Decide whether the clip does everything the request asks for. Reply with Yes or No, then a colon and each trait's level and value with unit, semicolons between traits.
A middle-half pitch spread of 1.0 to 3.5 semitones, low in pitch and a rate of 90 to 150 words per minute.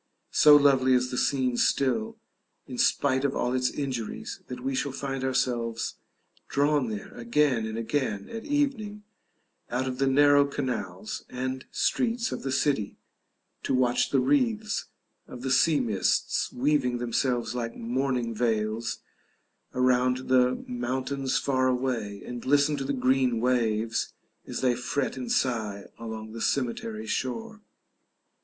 Yes: average, 2.7 semitones; low, 130 Hz; average, 140 wpm